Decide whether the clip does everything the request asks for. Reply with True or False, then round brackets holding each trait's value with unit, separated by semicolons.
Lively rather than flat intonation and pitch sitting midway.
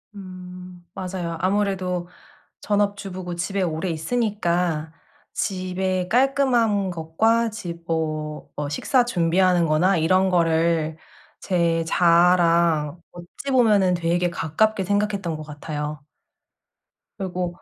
False (2.9 semitones; 180 Hz)